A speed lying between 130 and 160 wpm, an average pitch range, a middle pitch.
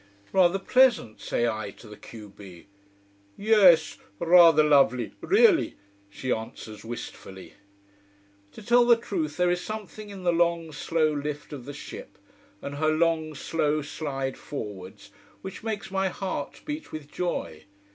No: average, 145 wpm; wide, 6.0 semitones; medium, 155 Hz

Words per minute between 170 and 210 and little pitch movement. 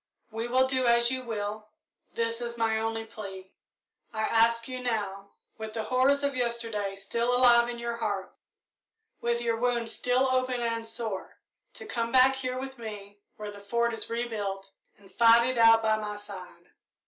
Yes: average, 175 wpm; narrow, 2.2 semitones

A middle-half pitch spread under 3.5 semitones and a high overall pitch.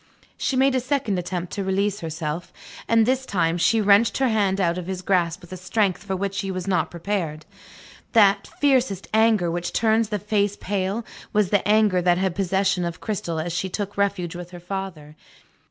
Yes: average, 3.0 semitones; high, 195 Hz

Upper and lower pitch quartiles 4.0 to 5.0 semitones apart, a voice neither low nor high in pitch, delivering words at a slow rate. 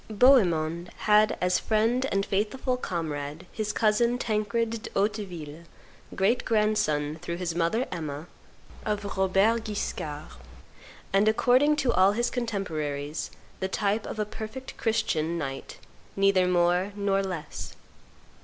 No: average, 4.5 semitones; high, 200 Hz; slow, 125 wpm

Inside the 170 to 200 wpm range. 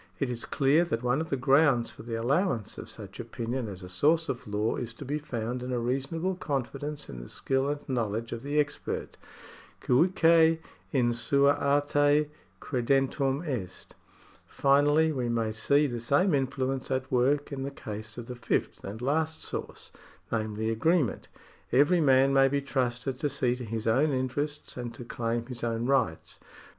Yes: average, 175 wpm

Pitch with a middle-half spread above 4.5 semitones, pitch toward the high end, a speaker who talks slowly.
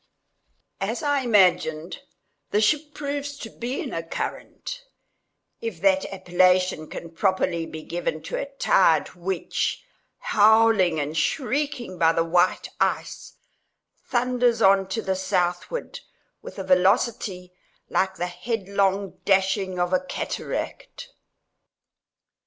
Yes: average, 5.0 semitones; high, 195 Hz; slow, 115 wpm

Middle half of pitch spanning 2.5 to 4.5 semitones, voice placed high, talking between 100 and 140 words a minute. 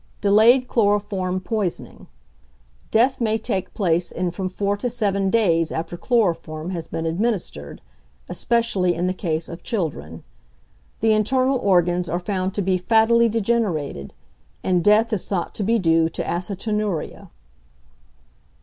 Yes: average, 4.2 semitones; high, 195 Hz; slow, 135 wpm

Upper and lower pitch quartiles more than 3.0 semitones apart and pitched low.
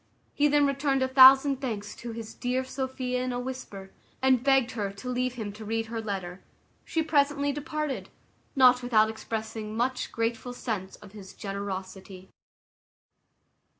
No: average, 3.7 semitones; high, 245 Hz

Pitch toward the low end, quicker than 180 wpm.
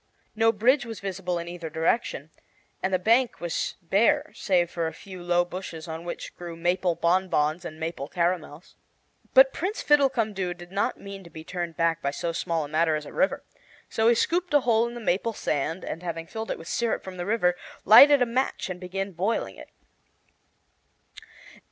No: medium, 180 Hz; average, 190 wpm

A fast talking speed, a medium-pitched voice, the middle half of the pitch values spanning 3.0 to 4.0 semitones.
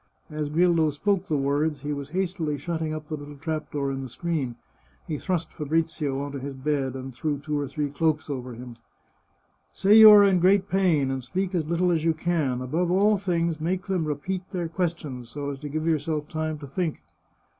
Yes: fast, 210 wpm; medium, 155 Hz; average, 3.5 semitones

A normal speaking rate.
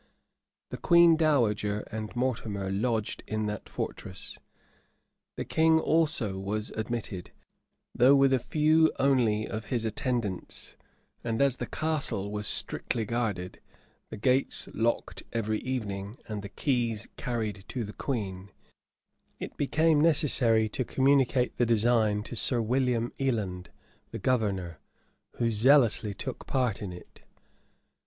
No: slow, 130 wpm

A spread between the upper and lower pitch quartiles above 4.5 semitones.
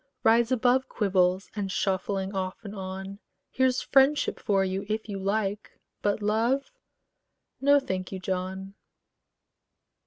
No: average, 3.3 semitones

